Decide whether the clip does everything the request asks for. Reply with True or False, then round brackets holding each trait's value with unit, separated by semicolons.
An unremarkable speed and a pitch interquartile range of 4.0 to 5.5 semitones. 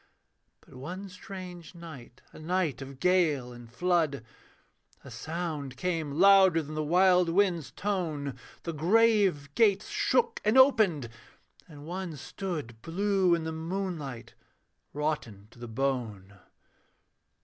False (125 wpm; 5.0 semitones)